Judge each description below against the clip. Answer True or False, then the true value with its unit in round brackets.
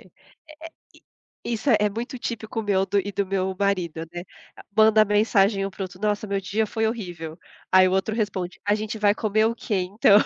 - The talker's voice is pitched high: True (205 Hz)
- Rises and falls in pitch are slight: True (2.3 semitones)